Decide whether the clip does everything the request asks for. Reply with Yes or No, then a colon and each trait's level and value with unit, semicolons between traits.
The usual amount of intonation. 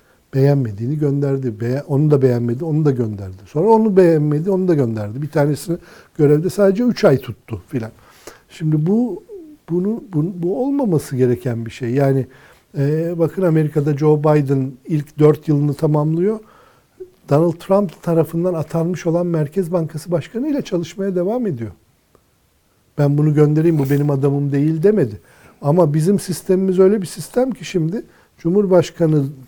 Yes: average, 4.4 semitones